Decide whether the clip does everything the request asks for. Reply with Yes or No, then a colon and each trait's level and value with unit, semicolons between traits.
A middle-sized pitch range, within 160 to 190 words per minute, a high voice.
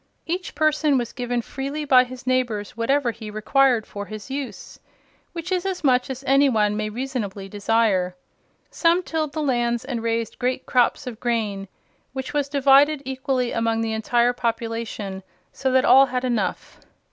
Yes: average, 3.3 semitones; average, 165 wpm; very high, 250 Hz